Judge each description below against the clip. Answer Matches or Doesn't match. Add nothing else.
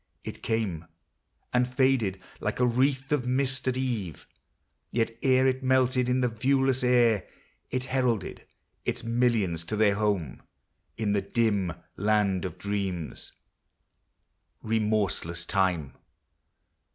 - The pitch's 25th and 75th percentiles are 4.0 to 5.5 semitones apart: Matches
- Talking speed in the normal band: Doesn't match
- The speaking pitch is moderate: Doesn't match